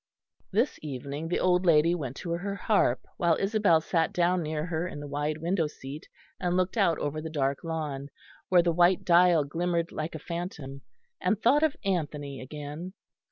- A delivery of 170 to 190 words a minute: Yes, average, 180 wpm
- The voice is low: No, medium, 165 Hz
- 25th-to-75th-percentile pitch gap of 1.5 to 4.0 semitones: Yes, average, 3.3 semitones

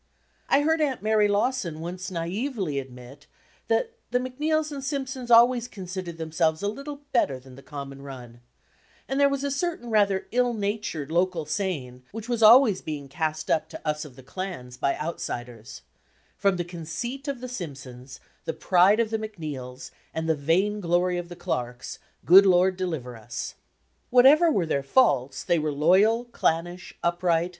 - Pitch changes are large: Yes, wide, 7.5 semitones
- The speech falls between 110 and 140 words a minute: No, average, 170 wpm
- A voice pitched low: No, medium, 180 Hz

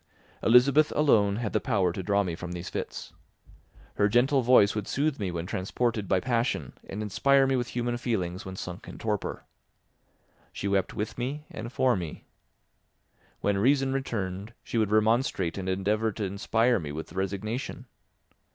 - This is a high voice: No, low, 105 Hz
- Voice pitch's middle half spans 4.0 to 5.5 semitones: Yes, average, 4.4 semitones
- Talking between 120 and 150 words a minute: No, average, 165 wpm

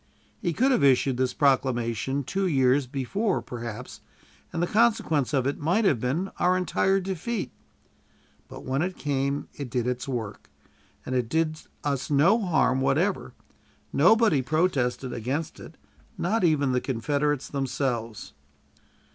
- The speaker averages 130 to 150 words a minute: Yes, average, 140 wpm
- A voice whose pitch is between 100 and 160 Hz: Yes, medium, 140 Hz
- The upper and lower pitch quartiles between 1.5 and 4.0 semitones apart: No, wide, 5.5 semitones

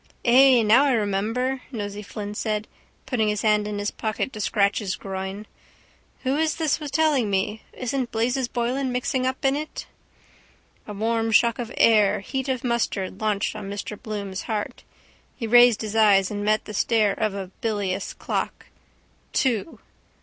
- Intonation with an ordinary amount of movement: Yes, average, 3.5 semitones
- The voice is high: Yes, high, 220 Hz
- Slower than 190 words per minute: Yes, average, 165 wpm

